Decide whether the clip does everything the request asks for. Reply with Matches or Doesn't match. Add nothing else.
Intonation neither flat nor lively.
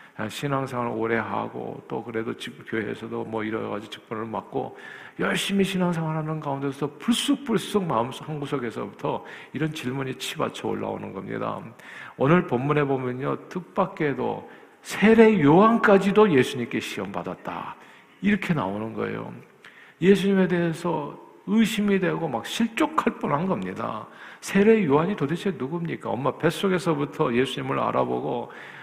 Doesn't match